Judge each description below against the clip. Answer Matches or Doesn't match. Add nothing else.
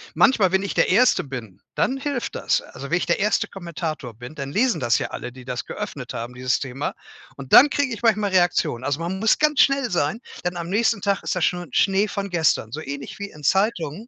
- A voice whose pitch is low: Doesn't match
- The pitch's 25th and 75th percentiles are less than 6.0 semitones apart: Doesn't match